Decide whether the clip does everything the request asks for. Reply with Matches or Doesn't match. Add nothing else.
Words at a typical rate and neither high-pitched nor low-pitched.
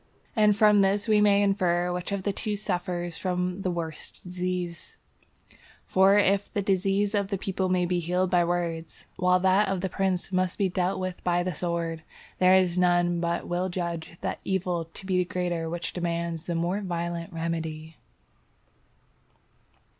Matches